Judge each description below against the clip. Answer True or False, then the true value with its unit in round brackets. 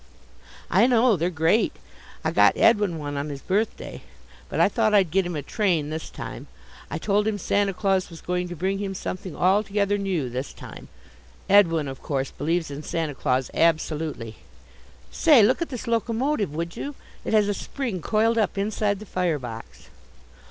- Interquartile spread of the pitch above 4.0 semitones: True (5.0 semitones)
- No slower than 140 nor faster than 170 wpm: False (180 wpm)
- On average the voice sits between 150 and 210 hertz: True (185 Hz)